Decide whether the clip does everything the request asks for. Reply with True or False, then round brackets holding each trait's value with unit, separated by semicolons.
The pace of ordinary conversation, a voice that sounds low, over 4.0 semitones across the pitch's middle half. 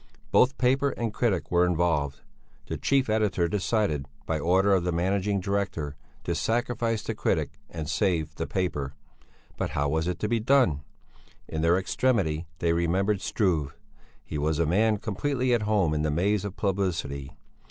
True (165 wpm; 90 Hz; 5.0 semitones)